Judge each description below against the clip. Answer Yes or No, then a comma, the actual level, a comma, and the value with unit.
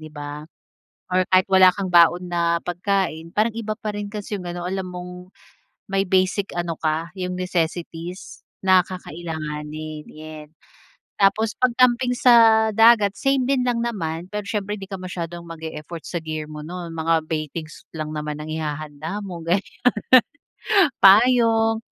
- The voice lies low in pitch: No, medium, 180 Hz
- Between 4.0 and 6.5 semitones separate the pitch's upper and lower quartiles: Yes, average, 4.3 semitones